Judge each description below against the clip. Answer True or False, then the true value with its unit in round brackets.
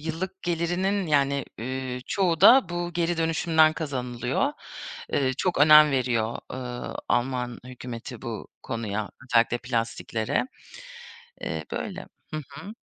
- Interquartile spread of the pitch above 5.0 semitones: True (5.4 semitones)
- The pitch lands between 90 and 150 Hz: True (140 Hz)